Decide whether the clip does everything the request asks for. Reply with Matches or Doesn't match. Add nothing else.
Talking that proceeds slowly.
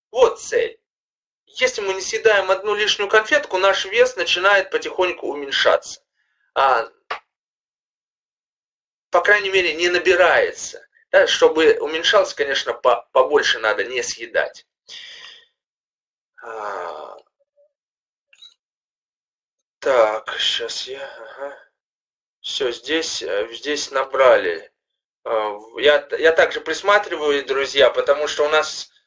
Matches